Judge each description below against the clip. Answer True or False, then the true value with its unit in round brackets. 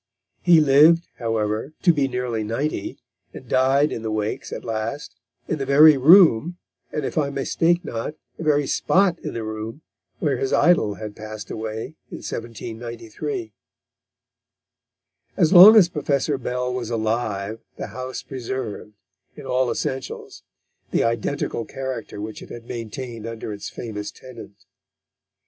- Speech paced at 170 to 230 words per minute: False (145 wpm)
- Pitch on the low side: True (125 Hz)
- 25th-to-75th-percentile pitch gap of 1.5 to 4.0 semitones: False (5.1 semitones)